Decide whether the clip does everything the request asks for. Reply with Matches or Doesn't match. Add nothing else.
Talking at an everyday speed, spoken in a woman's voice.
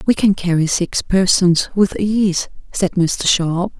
Matches